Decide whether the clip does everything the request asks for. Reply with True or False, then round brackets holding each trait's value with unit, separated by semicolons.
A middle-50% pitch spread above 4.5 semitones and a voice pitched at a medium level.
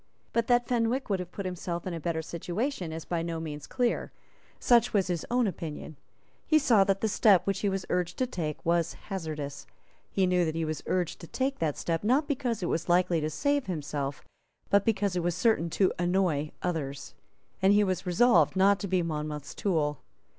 False (4.2 semitones; 180 Hz)